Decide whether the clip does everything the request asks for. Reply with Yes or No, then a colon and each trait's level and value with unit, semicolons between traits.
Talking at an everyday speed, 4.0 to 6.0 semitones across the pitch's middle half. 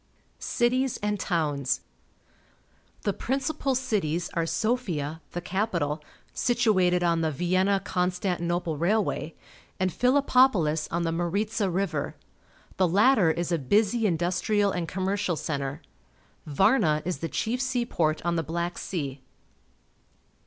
No: slow, 120 wpm; average, 4.6 semitones